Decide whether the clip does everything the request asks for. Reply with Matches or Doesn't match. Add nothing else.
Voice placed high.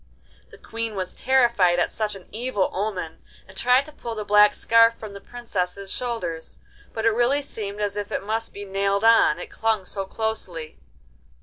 Matches